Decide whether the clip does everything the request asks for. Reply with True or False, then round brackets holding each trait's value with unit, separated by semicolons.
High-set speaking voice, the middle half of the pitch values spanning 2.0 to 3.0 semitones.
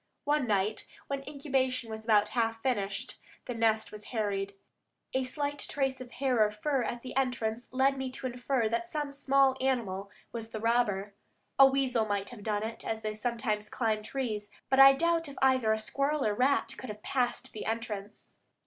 False (240 Hz; 3.8 semitones)